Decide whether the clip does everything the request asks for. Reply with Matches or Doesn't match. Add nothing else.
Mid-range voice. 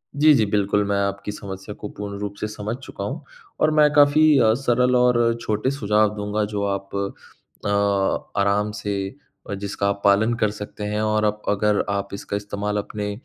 Doesn't match